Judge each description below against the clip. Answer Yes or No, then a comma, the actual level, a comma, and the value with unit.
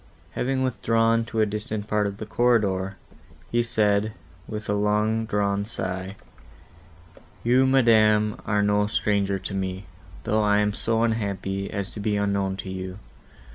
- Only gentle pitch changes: Yes, narrow, 2.0 semitones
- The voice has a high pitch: No, low, 105 Hz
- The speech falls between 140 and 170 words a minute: Yes, average, 150 wpm